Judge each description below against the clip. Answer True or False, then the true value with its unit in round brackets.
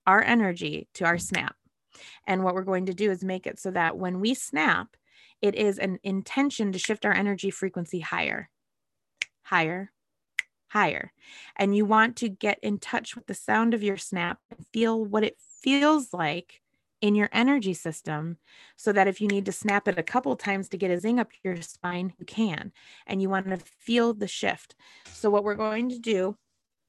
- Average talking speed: True (195 wpm)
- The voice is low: False (200 Hz)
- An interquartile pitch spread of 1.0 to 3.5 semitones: True (2.8 semitones)